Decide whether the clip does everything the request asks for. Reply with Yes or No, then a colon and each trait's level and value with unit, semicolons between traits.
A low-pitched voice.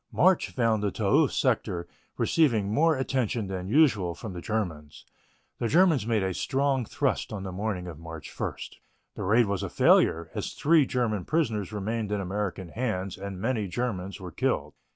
Yes: low, 105 Hz